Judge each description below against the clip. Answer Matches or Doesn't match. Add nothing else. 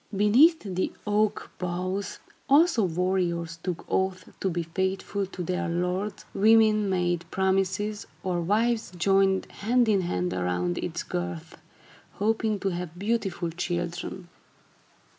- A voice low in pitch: Doesn't match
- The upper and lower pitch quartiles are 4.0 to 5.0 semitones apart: Doesn't match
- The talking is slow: Matches